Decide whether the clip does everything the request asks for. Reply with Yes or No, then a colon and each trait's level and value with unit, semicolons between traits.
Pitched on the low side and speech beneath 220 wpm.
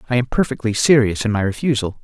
Yes: low, 115 Hz; fast, 205 wpm